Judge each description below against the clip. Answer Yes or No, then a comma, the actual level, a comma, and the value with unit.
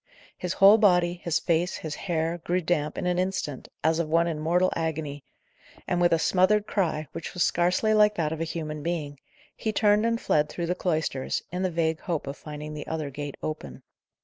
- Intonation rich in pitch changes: No, average, 2.8 semitones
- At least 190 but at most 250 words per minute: Yes, fast, 205 wpm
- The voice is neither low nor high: Yes, medium, 170 Hz